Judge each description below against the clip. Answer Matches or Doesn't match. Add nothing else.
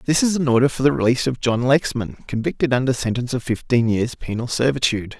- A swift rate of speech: Matches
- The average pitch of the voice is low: Matches